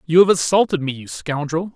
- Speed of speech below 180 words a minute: No, fast, 205 wpm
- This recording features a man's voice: Yes, male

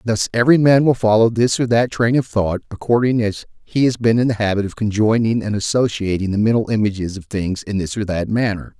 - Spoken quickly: Yes, fast, 225 wpm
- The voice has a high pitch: No, low, 110 Hz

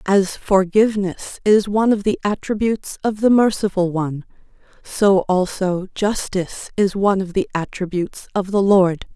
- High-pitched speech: Yes, high, 195 Hz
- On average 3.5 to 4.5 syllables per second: No, 4.9 syllables/s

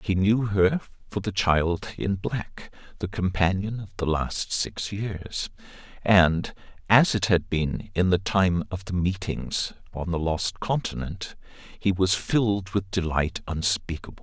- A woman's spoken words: No, male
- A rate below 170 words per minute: Yes, average, 150 wpm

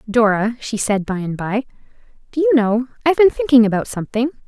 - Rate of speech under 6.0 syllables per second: No, 6.2 syllables/s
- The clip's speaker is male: No, female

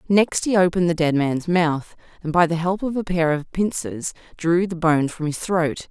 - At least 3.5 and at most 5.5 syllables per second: Yes, 4.8 syllables/s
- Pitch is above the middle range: No, medium, 170 Hz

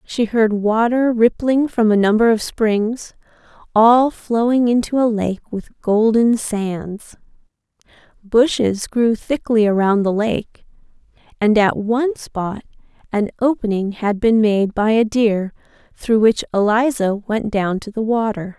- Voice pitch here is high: Yes, high, 220 Hz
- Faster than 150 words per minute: No, average, 140 wpm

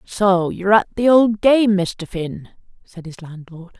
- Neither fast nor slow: Yes, average, 175 wpm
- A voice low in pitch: No, high, 195 Hz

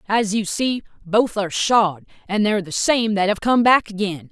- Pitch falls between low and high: No, high, 205 Hz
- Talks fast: Yes, fast, 210 wpm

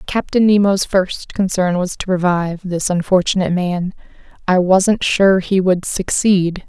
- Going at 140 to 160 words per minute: Yes, average, 145 wpm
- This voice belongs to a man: No, female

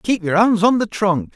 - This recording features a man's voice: Yes, male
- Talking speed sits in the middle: No, fast, 265 wpm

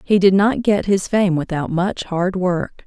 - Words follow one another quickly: Yes, fast, 210 wpm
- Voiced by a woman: Yes, female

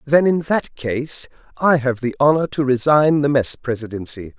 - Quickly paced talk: No, average, 180 wpm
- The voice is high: No, medium, 140 Hz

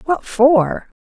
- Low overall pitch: No, very high, 265 Hz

